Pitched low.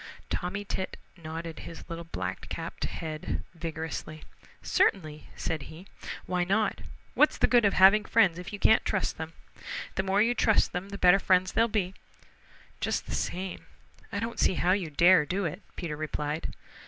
No: medium, 180 Hz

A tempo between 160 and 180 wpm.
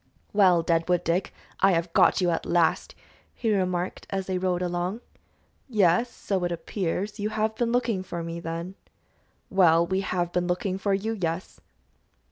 Yes: average, 165 wpm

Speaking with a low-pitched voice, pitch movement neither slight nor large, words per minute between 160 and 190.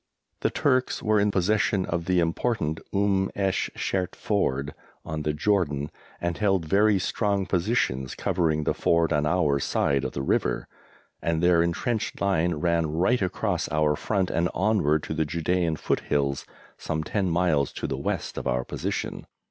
Yes: very low, 85 Hz; average, 4.3 semitones; average, 165 wpm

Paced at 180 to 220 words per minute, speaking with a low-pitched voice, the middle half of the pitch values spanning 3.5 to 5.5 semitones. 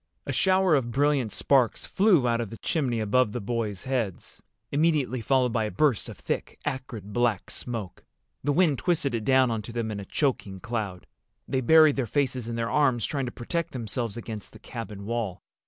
Yes: average, 190 wpm; low, 120 Hz; average, 3.8 semitones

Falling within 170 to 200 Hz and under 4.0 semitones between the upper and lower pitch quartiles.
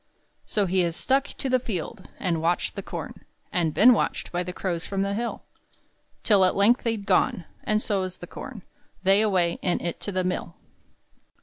Yes: high, 190 Hz; average, 3.3 semitones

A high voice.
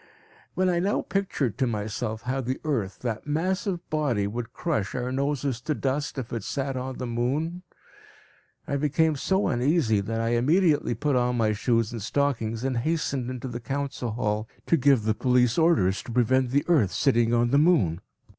No: low, 130 Hz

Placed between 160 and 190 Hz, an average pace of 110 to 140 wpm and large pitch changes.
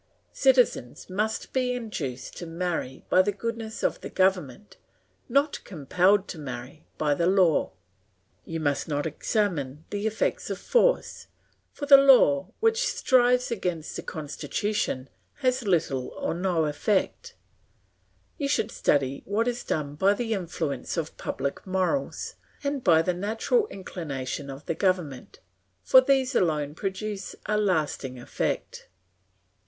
Yes: medium, 185 Hz; slow, 135 wpm; wide, 7.3 semitones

